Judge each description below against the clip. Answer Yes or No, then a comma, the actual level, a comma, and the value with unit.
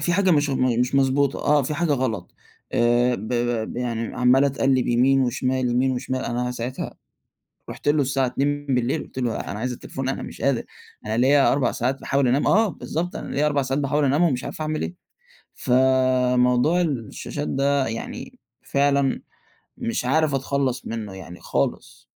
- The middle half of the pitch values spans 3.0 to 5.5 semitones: No, narrow, 2.4 semitones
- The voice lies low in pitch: Yes, low, 130 Hz